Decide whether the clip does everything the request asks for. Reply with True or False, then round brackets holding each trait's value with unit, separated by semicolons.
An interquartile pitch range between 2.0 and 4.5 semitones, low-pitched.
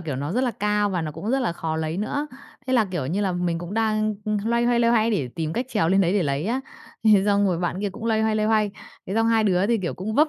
False (4.2 semitones; 205 Hz)